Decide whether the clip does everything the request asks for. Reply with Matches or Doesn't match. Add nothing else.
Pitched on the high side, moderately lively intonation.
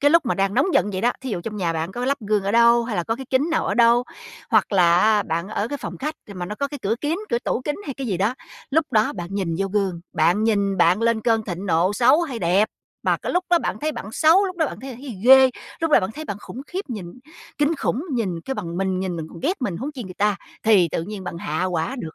Doesn't match